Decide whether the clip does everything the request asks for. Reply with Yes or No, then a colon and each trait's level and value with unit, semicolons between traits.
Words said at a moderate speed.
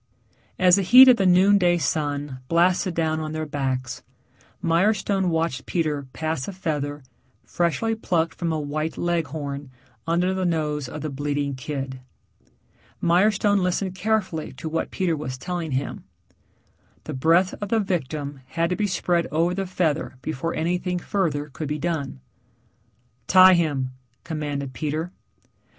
Yes: average, 145 wpm